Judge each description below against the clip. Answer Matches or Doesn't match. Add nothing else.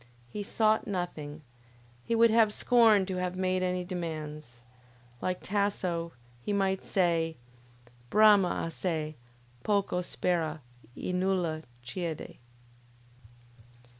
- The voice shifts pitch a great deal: Doesn't match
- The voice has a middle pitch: Matches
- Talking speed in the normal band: Doesn't match